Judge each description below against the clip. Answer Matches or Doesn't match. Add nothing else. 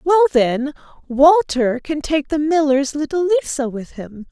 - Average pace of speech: Matches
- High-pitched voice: Matches